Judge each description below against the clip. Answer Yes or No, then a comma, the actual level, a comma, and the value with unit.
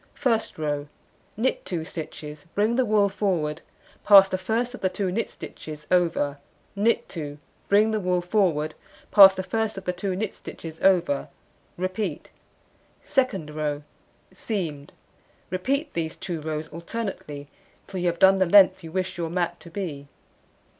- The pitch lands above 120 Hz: Yes, medium, 185 Hz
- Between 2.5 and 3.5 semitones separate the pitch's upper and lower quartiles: No, average, 4.3 semitones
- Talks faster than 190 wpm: No, average, 155 wpm